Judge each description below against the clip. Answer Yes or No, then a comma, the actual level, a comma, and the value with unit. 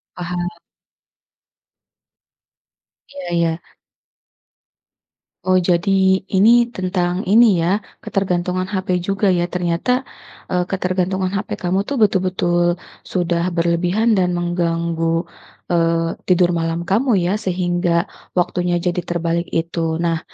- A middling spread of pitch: No, narrow, 1.8 semitones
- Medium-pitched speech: Yes, medium, 175 Hz